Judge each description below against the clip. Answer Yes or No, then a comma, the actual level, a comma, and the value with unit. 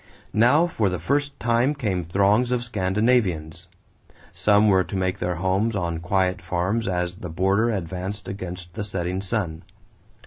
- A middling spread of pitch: Yes, average, 3.7 semitones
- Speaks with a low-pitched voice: Yes, very low, 95 Hz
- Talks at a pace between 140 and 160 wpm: Yes, average, 150 wpm